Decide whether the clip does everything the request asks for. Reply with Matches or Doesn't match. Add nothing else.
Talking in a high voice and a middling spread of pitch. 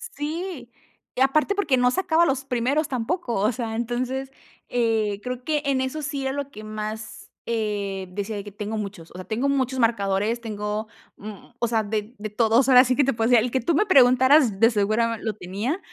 Matches